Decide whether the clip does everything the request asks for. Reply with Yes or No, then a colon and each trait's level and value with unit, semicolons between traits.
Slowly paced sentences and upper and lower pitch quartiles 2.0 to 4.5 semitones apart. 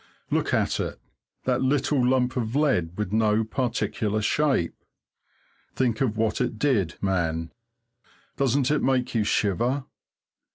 Yes: slow, 130 wpm; average, 3.8 semitones